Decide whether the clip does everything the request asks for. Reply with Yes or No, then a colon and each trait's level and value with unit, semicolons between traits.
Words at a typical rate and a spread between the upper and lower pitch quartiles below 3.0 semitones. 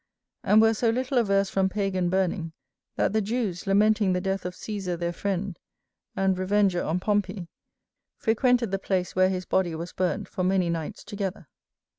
Yes: average, 170 wpm; narrow, 2.4 semitones